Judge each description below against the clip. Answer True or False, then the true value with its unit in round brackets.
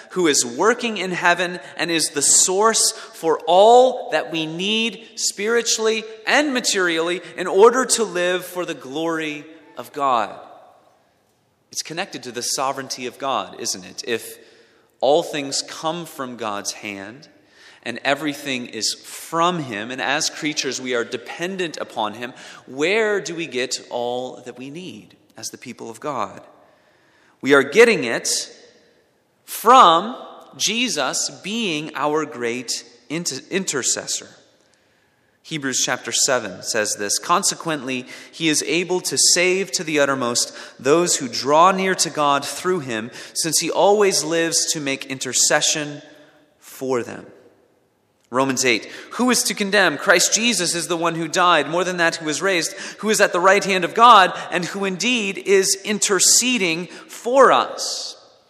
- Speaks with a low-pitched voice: False (165 Hz)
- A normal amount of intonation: False (5.8 semitones)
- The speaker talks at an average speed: True (150 wpm)